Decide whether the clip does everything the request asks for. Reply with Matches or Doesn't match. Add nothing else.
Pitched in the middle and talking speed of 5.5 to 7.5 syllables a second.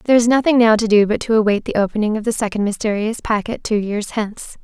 Doesn't match